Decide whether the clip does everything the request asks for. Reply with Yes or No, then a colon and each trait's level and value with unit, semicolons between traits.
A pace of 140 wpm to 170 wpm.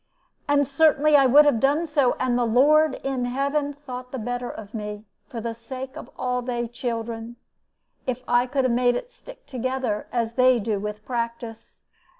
No: average, 180 wpm